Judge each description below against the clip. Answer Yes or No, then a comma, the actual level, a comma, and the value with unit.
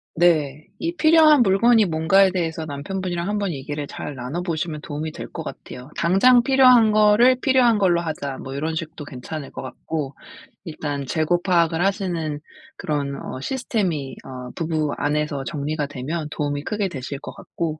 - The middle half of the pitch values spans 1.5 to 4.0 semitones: No, average, 5.1 semitones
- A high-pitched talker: No, medium, 160 Hz